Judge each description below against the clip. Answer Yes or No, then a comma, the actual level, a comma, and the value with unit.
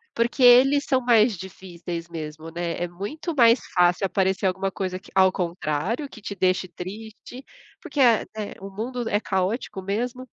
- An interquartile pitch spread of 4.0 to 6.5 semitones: Yes, average, 4.7 semitones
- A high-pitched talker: Yes, high, 195 Hz